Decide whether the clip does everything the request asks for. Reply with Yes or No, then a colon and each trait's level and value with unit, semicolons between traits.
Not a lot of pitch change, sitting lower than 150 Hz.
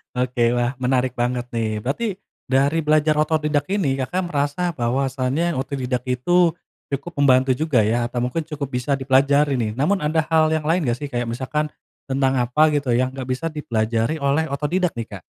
No: average, 3.5 semitones; low, 135 Hz